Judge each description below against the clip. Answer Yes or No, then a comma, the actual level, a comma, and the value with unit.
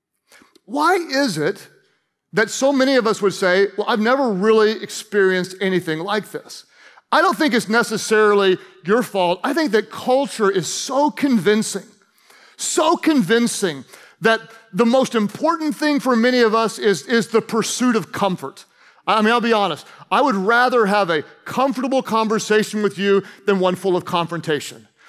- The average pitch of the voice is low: No, high, 220 Hz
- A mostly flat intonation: No, average, 4.1 semitones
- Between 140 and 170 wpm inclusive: Yes, average, 165 wpm